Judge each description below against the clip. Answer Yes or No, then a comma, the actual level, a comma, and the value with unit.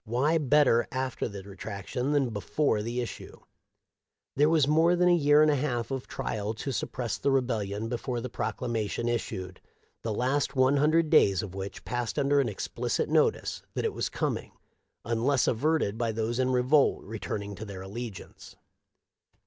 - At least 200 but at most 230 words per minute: No, average, 175 wpm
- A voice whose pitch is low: Yes, low, 120 Hz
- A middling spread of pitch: Yes, average, 4.6 semitones